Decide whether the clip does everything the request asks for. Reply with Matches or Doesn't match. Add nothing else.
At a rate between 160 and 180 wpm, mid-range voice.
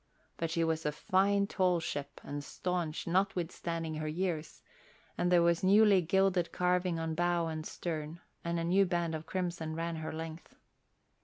Matches